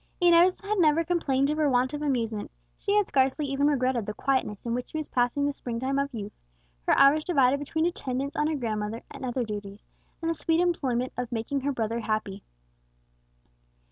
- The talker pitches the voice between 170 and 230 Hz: No, very high, 270 Hz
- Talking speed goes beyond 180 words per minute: Yes, average, 195 wpm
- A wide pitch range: No, average, 4.3 semitones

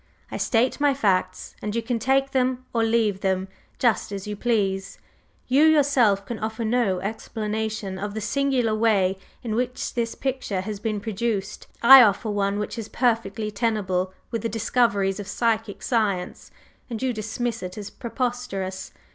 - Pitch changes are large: No, average, 3.1 semitones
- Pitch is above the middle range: Yes, high, 220 Hz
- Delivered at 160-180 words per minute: Yes, average, 165 wpm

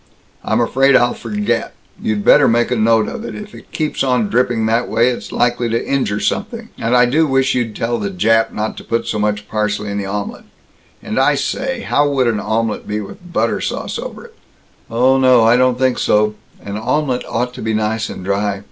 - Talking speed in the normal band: No, fast, 220 wpm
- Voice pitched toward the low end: Yes, low, 115 Hz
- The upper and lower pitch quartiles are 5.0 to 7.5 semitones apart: No, average, 3.7 semitones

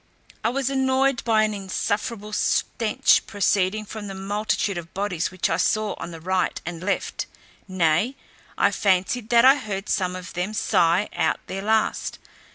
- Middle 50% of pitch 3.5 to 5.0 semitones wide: No, average, 3.1 semitones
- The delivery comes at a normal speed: Yes, average, 165 wpm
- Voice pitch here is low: No, high, 205 Hz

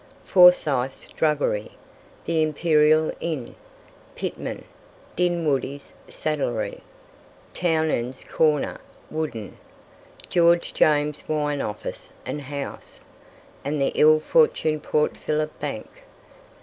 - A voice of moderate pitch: Yes, medium, 150 Hz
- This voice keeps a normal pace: No, slow, 85 wpm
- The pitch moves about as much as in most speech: No, narrow, 2.0 semitones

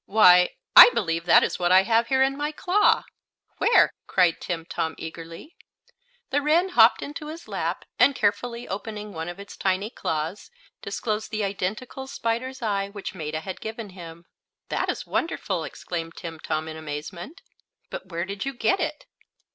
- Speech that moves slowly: No, average, 165 wpm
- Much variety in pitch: Yes, wide, 6.4 semitones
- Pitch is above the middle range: Yes, high, 200 Hz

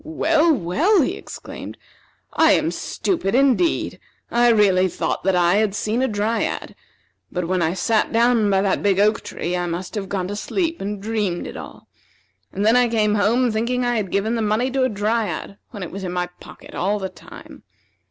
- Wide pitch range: No, average, 3.9 semitones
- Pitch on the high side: Yes, high, 210 Hz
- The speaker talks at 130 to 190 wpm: No, average, 200 wpm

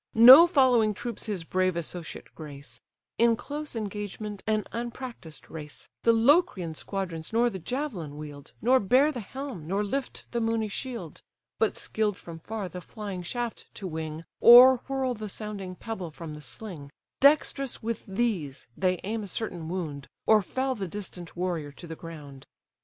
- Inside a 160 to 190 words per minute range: Yes, average, 165 wpm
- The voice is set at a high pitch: Yes, high, 205 Hz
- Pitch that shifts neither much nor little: No, wide, 6.1 semitones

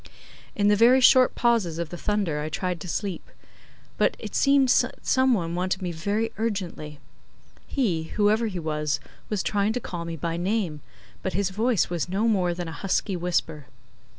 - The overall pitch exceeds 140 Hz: Yes, medium, 185 Hz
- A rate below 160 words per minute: No, average, 180 wpm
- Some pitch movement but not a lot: Yes, average, 4.5 semitones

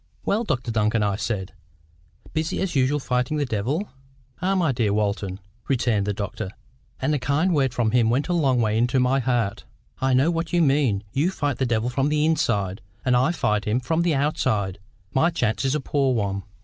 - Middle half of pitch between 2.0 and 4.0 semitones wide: No, wide, 5.4 semitones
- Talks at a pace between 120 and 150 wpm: No, average, 200 wpm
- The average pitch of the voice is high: No, low, 130 Hz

